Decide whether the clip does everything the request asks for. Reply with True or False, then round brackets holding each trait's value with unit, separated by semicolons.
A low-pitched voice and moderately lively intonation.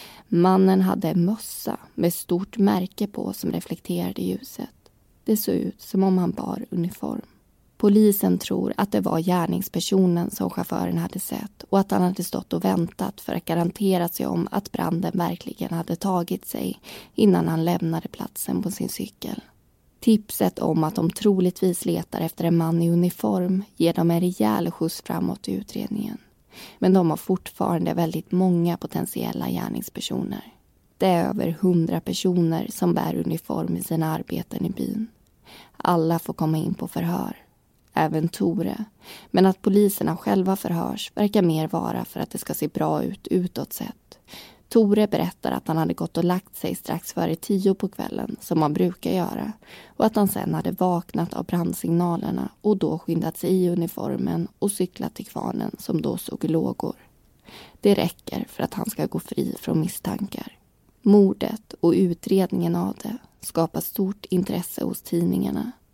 False (180 Hz; 3.2 semitones)